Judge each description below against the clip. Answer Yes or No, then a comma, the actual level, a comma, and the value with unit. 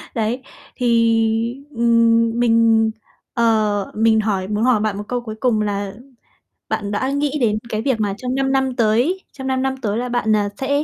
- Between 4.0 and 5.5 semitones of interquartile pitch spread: No, average, 2.7 semitones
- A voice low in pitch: No, high, 230 Hz